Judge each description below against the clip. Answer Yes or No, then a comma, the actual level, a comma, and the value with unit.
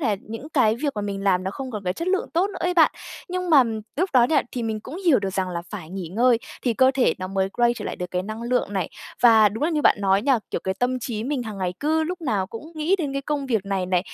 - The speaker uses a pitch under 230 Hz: No, high, 235 Hz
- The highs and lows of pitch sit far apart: Yes, wide, 6.7 semitones